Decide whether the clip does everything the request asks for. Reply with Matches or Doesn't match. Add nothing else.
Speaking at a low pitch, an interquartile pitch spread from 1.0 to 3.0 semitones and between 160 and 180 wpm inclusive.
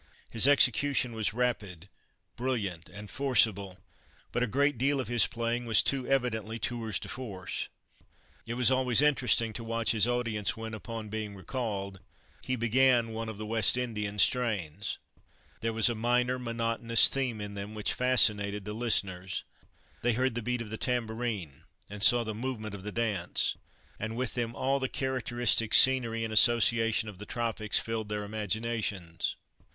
Matches